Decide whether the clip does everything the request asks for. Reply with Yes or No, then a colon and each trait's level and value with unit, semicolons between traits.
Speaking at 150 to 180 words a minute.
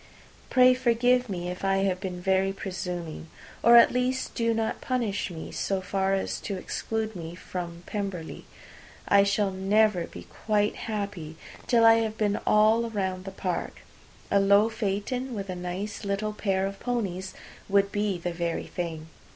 Yes: average, 165 wpm